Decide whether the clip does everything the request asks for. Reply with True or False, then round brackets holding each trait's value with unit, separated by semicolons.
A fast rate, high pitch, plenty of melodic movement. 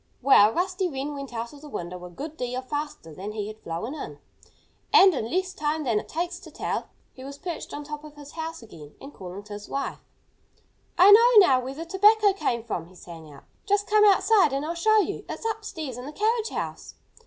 True (225 wpm; 290 Hz; 8.5 semitones)